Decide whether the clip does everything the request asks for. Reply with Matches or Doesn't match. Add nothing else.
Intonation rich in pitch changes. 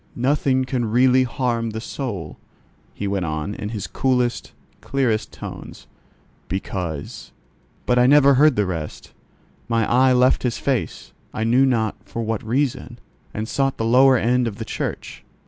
Doesn't match